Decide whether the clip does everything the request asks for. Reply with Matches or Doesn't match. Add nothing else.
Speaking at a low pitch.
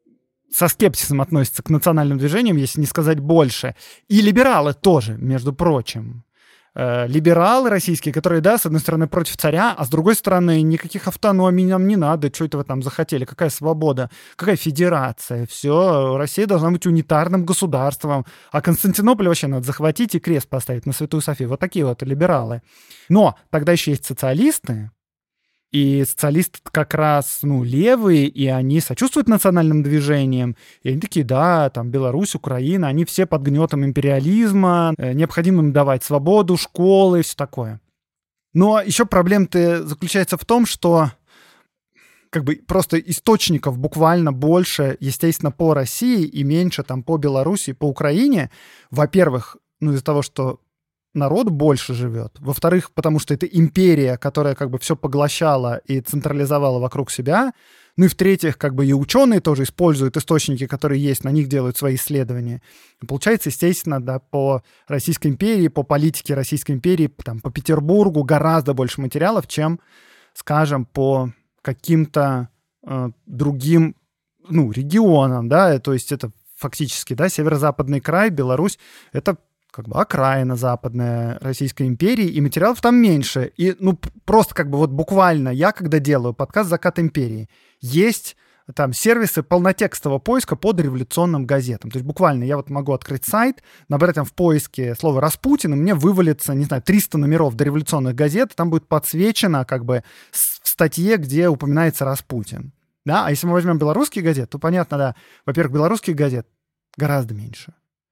Doesn't match